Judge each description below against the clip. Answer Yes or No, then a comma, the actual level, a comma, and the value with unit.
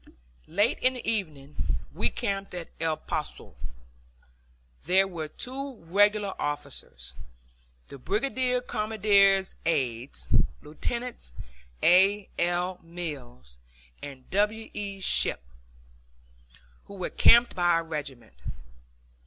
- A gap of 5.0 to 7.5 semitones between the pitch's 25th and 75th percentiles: Yes, wide, 5.5 semitones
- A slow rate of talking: Yes, slow, 100 wpm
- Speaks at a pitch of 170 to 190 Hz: Yes, medium, 185 Hz